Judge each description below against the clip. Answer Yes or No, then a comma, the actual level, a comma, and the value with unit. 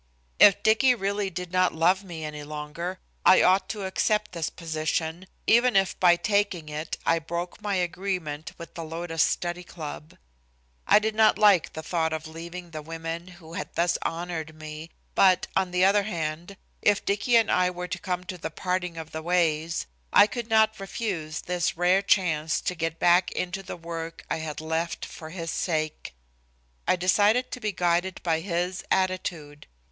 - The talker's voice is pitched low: No, medium, 175 Hz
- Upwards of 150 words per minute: Yes, average, 180 wpm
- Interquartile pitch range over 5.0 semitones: No, average, 2.8 semitones